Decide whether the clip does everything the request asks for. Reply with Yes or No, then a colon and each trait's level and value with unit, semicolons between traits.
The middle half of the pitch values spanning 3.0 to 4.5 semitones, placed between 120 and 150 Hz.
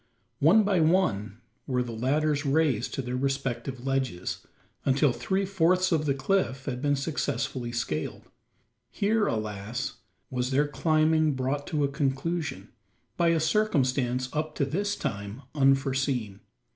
Yes: average, 4.0 semitones; low, 135 Hz